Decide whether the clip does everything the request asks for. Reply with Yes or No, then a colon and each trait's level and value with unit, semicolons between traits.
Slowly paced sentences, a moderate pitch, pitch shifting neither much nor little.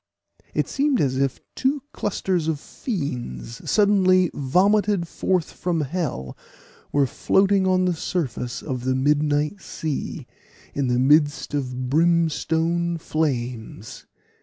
No: slow, 115 wpm; medium, 155 Hz; wide, 5.8 semitones